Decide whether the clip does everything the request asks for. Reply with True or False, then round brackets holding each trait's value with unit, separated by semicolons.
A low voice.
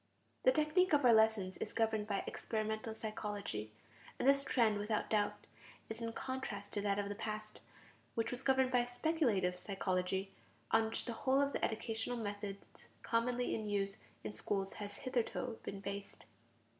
False (220 Hz)